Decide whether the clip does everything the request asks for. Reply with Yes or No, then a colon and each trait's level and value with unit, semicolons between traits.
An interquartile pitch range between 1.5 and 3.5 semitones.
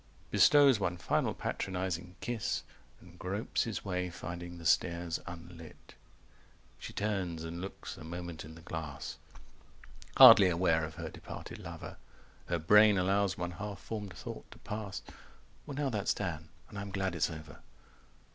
Yes: average, 3.0 semitones